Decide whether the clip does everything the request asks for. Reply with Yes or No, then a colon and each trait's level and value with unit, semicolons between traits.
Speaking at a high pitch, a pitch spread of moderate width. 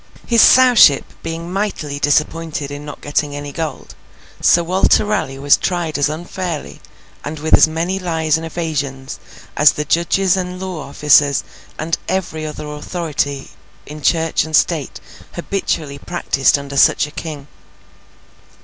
No: medium, 155 Hz; average, 3.0 semitones